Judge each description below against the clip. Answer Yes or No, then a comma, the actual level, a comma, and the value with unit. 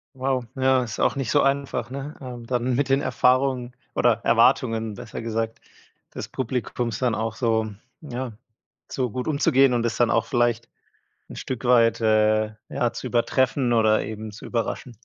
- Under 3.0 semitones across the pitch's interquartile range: Yes, narrow, 2.5 semitones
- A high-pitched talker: No, low, 120 Hz